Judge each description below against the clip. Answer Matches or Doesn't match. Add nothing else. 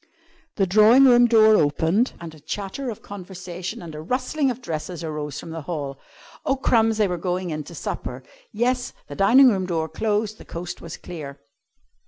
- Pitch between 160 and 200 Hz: Matches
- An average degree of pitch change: Doesn't match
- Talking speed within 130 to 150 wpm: Doesn't match